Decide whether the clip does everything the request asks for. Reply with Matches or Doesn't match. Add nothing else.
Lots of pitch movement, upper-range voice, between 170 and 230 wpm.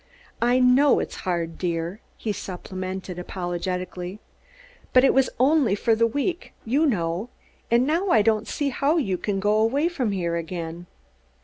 Doesn't match